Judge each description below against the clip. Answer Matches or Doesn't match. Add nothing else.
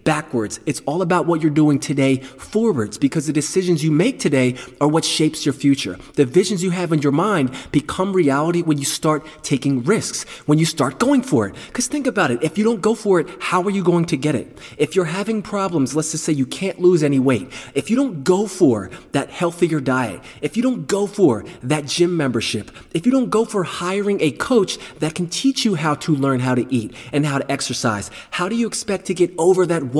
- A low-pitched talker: Doesn't match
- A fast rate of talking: Matches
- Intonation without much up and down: Doesn't match